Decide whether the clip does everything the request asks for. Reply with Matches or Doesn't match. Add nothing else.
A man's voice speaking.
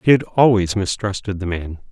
Matches